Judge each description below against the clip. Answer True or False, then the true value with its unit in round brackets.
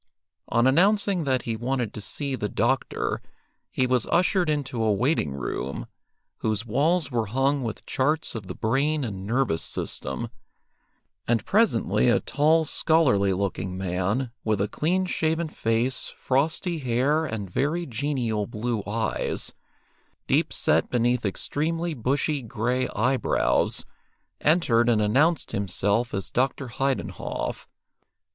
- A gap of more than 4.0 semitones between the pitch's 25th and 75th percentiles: True (5.5 semitones)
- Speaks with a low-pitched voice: True (125 Hz)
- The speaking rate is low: True (130 wpm)